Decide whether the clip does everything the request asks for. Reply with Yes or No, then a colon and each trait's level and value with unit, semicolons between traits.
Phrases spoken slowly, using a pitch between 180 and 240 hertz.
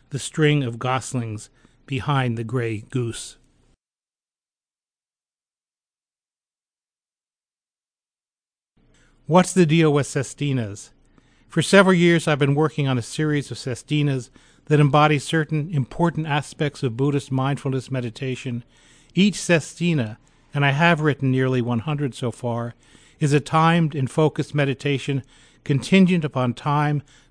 No: slow, 115 wpm; medium, 140 Hz